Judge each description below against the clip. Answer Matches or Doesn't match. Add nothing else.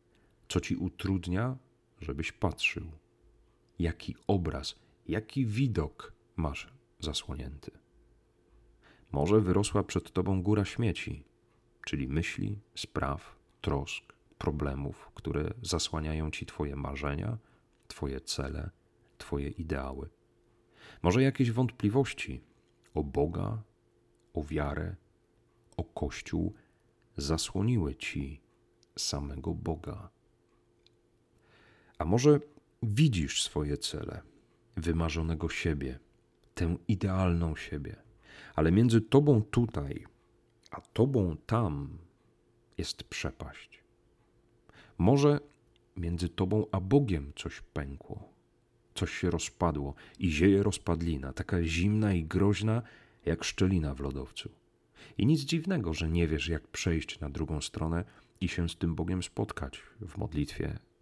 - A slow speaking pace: Matches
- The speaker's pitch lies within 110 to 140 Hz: Doesn't match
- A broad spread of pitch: Matches